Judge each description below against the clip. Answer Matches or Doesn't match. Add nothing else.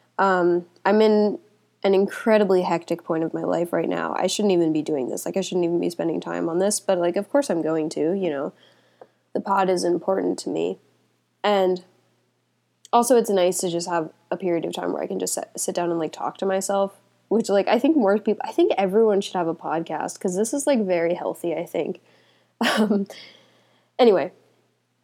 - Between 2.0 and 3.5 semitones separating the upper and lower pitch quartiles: Matches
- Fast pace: Matches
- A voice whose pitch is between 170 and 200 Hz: Matches